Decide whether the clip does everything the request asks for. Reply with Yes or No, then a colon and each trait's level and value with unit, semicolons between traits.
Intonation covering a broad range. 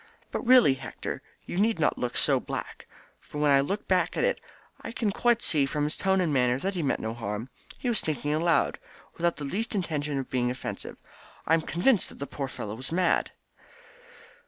Yes: wide, 6.1 semitones